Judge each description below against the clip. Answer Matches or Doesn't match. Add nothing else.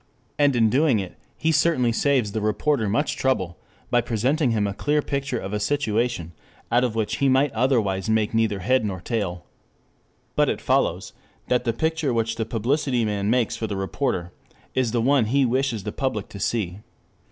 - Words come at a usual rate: Matches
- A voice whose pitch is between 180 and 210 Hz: Doesn't match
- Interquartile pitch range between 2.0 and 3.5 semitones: Doesn't match